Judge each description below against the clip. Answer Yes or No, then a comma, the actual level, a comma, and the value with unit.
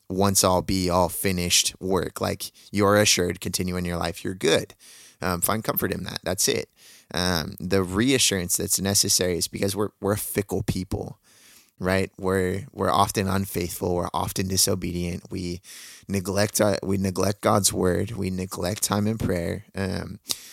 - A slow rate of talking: No, average, 160 wpm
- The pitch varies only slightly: Yes, narrow, 1.8 semitones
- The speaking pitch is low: Yes, very low, 95 Hz